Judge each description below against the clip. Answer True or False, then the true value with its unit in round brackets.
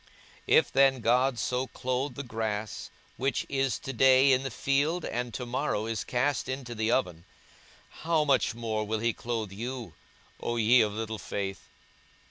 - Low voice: True (120 Hz)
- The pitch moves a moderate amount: True (3.3 semitones)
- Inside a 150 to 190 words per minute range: True (170 wpm)